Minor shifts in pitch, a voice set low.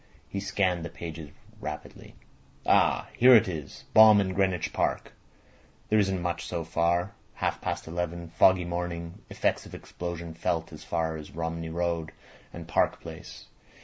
Yes: narrow, 1.8 semitones; very low, 85 Hz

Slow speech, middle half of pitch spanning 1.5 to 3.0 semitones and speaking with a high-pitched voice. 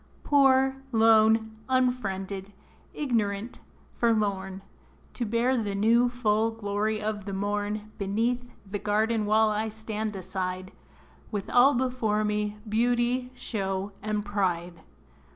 Yes: slow, 115 wpm; narrow, 2.6 semitones; high, 215 Hz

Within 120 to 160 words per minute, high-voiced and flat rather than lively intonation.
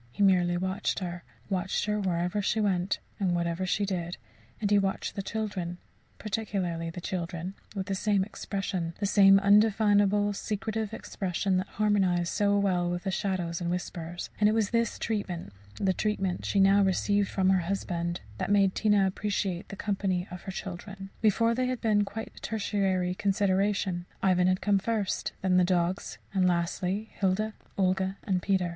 No: average, 170 wpm; high, 195 Hz; narrow, 2.3 semitones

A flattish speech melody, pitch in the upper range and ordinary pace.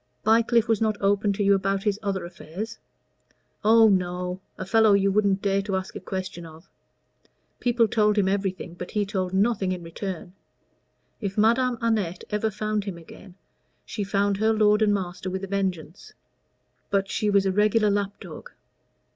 Yes: narrow, 2.0 semitones; high, 200 Hz; average, 170 wpm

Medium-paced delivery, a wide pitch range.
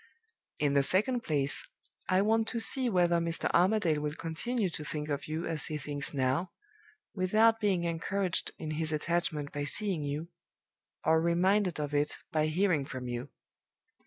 No: average, 160 wpm; average, 4.3 semitones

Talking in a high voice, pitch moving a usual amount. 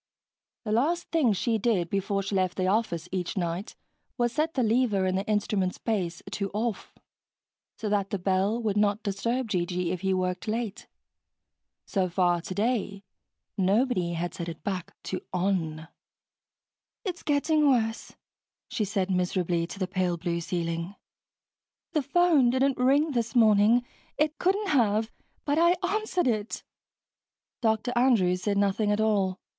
Yes: high, 205 Hz; average, 4.6 semitones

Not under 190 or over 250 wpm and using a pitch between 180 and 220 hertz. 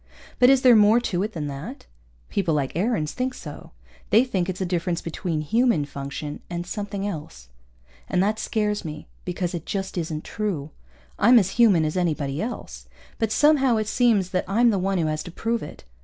Yes: average, 195 wpm; medium, 185 Hz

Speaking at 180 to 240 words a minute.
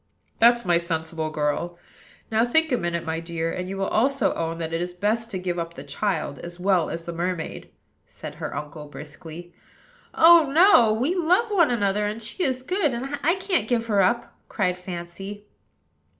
Yes: average, 190 wpm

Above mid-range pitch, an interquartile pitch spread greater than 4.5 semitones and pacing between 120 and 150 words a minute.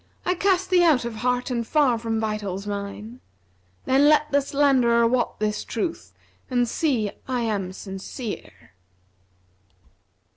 Yes: high, 235 Hz; average, 4.9 semitones; average, 140 wpm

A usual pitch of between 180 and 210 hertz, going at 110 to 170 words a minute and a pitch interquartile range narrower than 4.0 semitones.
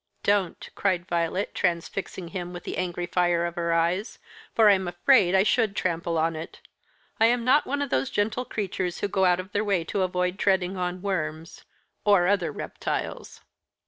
No: medium, 185 Hz; average, 180 wpm; average, 2.7 semitones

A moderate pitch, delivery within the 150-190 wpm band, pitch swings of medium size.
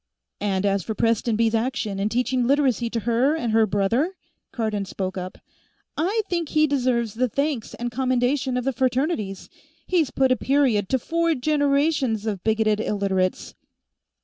No: high, 240 Hz; average, 160 wpm; average, 4.6 semitones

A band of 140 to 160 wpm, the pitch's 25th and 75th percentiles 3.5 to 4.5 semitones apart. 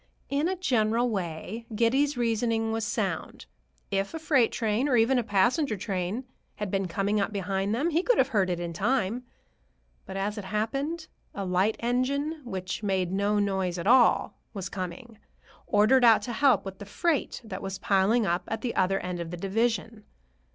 No: average, 180 wpm; average, 4.2 semitones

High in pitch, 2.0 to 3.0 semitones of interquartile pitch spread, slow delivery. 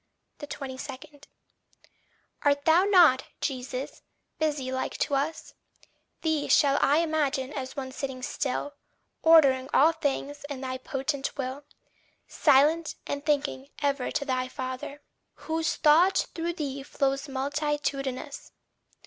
Yes: very high, 280 Hz; narrow, 2.4 semitones; slow, 115 wpm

